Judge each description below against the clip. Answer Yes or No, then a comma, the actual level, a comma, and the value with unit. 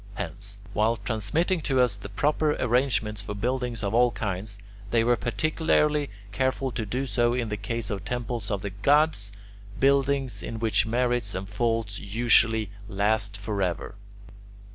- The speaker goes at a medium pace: Yes, average, 150 wpm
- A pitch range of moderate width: Yes, average, 3.7 semitones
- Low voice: Yes, low, 115 Hz